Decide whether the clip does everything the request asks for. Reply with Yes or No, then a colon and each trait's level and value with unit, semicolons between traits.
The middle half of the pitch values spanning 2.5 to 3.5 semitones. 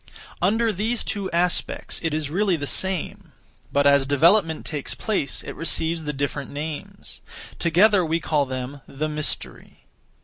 No: average, 4.5 semitones